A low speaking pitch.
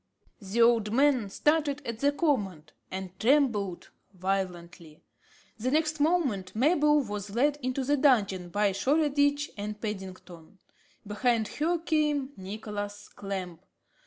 No: high, 225 Hz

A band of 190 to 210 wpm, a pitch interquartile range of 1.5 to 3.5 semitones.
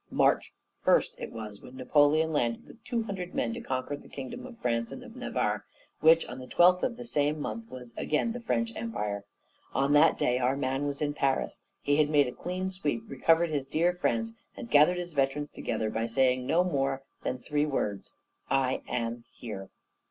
No: average, 195 wpm; wide, 5.4 semitones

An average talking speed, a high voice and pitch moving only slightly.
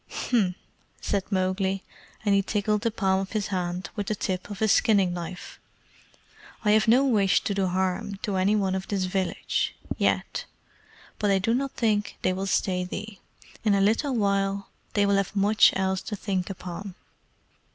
Yes: average, 180 wpm; high, 195 Hz; narrow, 1.9 semitones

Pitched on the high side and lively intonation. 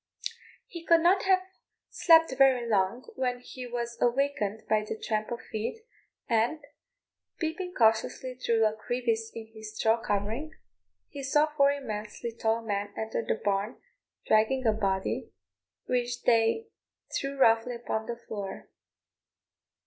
No: high, 235 Hz; average, 3.8 semitones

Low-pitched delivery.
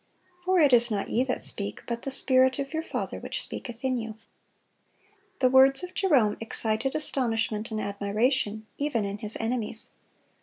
No: high, 245 Hz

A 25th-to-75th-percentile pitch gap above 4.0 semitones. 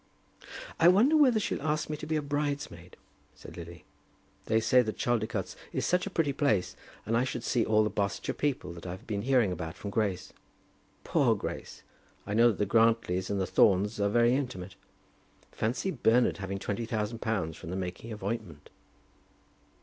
Yes: average, 5.2 semitones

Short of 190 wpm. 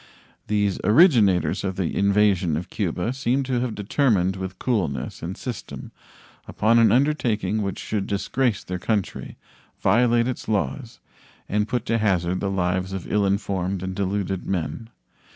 Yes: average, 150 wpm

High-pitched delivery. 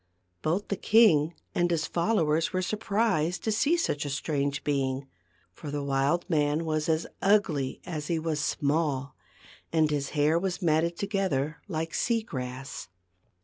No: medium, 160 Hz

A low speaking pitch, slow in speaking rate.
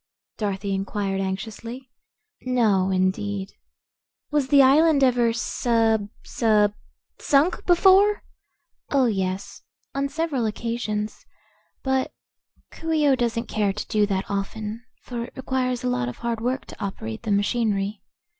No: high, 230 Hz; slow, 130 wpm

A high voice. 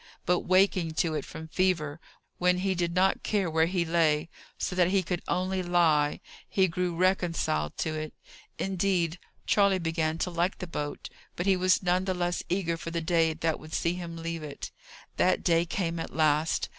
No: medium, 170 Hz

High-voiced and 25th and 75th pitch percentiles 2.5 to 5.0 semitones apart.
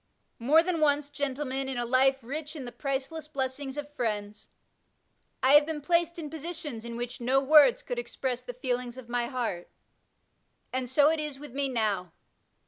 Yes: very high, 270 Hz; average, 3.3 semitones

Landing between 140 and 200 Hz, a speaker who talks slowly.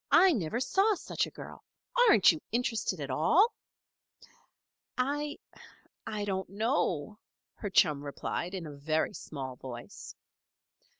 Yes: high, 190 Hz; slow, 125 wpm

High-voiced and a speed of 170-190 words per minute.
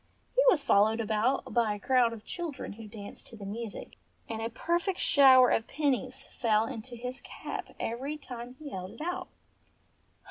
Yes: high, 240 Hz; average, 175 wpm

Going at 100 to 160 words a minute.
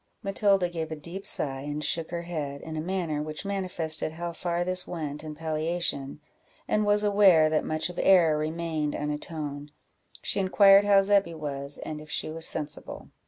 No: average, 175 wpm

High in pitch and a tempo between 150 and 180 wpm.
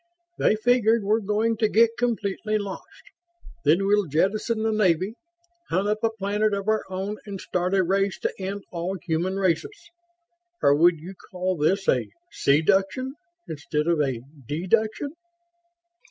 Yes: high, 195 Hz; average, 155 wpm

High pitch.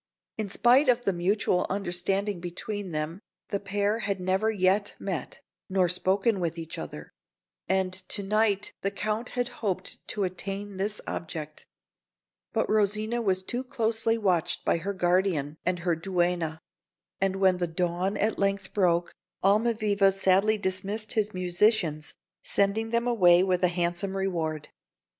Yes: high, 195 Hz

